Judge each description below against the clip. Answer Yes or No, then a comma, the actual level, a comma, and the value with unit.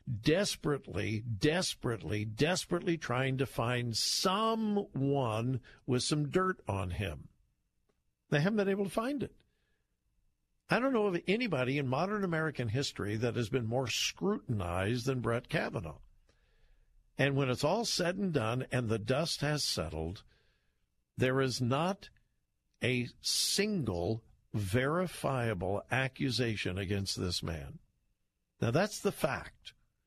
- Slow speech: Yes, slow, 125 wpm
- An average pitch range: No, wide, 6.5 semitones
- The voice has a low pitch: Yes, low, 130 Hz